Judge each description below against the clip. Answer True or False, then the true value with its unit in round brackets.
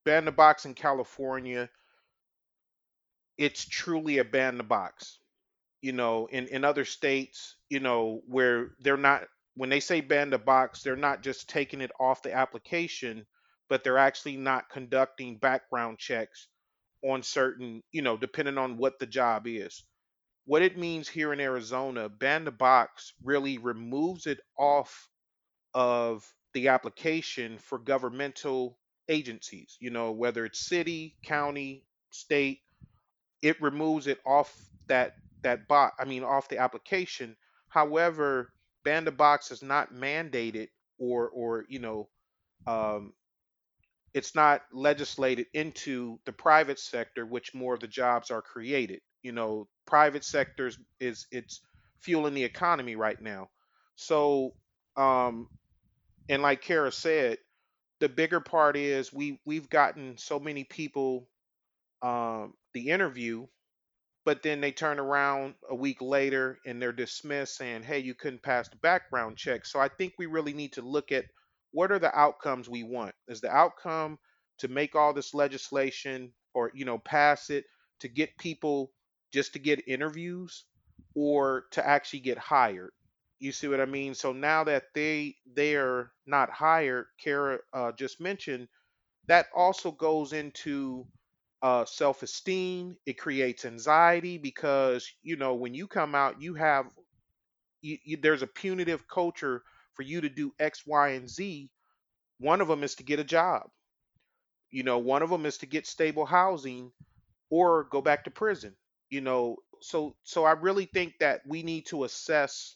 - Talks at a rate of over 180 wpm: False (155 wpm)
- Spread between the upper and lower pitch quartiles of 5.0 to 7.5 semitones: False (3.4 semitones)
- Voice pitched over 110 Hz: True (140 Hz)